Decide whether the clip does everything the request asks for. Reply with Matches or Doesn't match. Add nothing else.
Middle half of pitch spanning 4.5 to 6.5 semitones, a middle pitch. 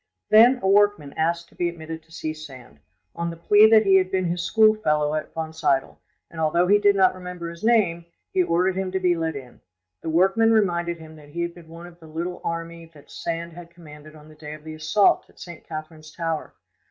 Doesn't match